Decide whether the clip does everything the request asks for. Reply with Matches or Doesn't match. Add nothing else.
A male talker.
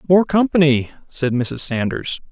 Matches